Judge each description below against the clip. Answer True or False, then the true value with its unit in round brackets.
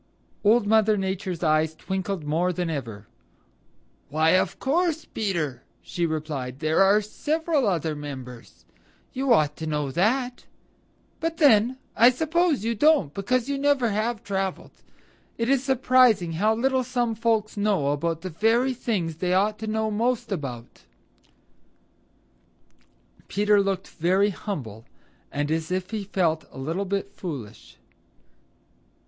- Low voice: False (195 Hz)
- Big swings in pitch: True (6.6 semitones)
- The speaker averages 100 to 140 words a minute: True (135 wpm)